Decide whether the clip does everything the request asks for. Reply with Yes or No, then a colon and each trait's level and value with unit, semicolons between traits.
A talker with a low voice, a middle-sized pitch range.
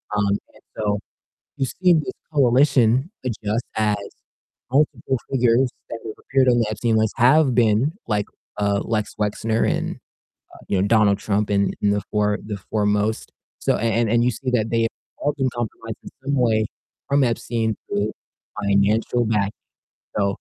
Yes: low, 110 Hz; average, 3.2 semitones